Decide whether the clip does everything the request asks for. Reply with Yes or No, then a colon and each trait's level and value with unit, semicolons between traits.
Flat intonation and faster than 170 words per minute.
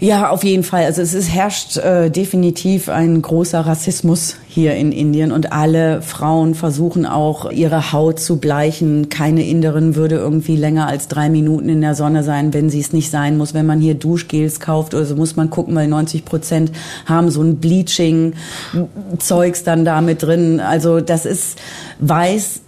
Yes: narrow, 1.7 semitones; average, 180 wpm